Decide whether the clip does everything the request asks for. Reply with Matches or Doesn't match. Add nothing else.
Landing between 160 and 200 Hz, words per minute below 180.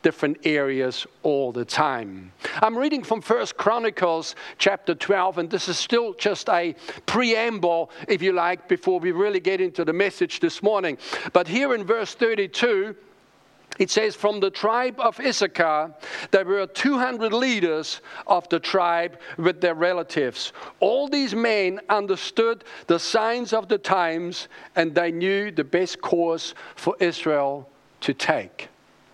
Matches